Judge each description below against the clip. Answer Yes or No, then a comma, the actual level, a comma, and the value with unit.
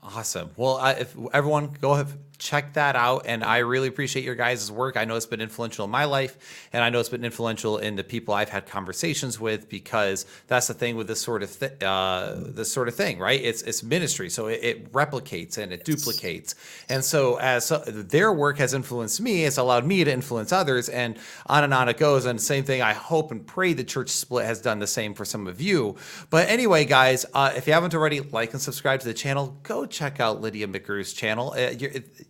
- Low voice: Yes, low, 125 Hz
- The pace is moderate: No, fast, 230 wpm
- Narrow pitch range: No, average, 3.9 semitones